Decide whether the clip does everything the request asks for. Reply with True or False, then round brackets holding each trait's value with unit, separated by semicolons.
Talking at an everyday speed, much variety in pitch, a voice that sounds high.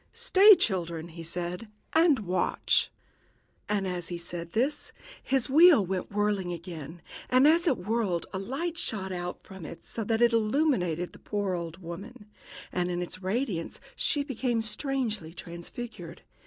True (155 wpm; 6.2 semitones; 200 Hz)